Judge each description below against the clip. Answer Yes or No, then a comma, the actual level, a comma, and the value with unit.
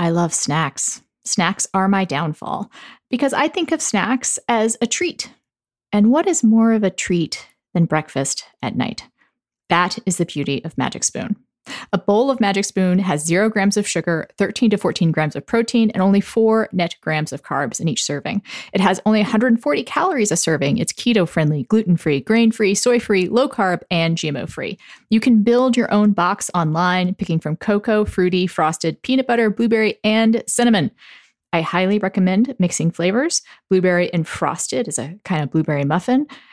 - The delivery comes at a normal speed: Yes, average, 180 wpm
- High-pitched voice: Yes, high, 200 Hz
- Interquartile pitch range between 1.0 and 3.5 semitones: No, average, 4.9 semitones